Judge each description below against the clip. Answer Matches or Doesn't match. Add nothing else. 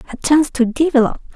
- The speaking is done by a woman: Matches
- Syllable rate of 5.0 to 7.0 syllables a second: Doesn't match